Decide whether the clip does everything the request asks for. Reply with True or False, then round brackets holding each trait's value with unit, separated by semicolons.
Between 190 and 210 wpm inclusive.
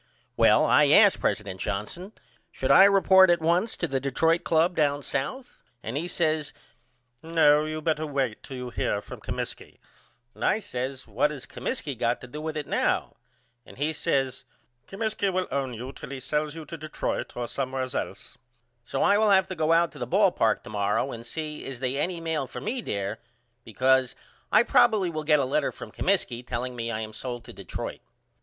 True (200 wpm)